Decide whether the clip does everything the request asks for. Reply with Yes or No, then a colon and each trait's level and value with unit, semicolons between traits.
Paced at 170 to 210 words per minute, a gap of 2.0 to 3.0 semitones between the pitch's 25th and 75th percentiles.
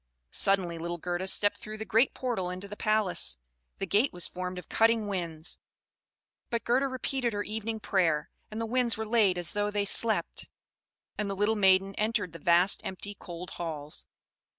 No: average, 175 wpm; average, 3.7 semitones